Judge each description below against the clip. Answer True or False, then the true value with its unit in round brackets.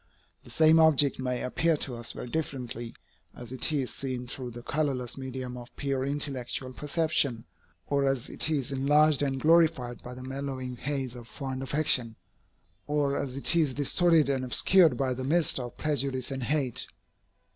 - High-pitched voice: False (135 Hz)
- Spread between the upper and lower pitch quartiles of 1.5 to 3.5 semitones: True (2.7 semitones)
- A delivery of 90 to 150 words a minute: False (165 wpm)